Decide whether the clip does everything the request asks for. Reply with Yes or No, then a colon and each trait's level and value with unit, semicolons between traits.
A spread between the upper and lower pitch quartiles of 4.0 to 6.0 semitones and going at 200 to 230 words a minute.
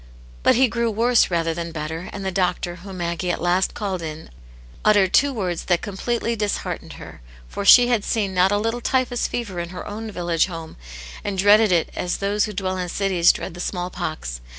No: average, 3.4 semitones; fast, 205 wpm